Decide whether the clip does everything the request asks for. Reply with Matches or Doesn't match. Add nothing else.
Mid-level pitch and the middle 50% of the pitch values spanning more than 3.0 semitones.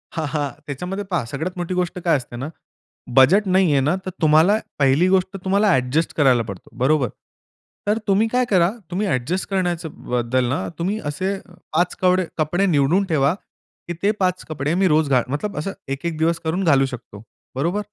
Matches